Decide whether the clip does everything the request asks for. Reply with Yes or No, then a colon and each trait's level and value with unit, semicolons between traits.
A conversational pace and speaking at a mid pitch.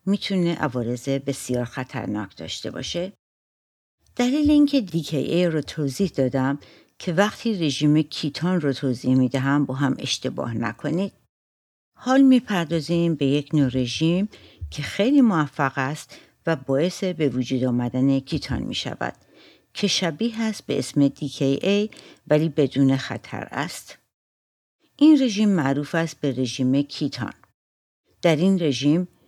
No: slow, 125 wpm; medium, 145 Hz